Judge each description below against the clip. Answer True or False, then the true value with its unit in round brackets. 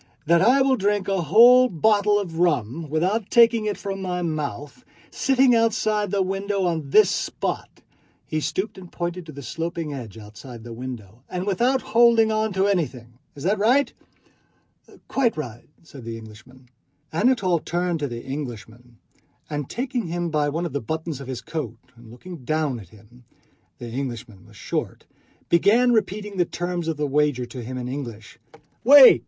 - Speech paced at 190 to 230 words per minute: False (170 wpm)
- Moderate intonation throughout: False (8.2 semitones)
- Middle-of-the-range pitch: True (165 Hz)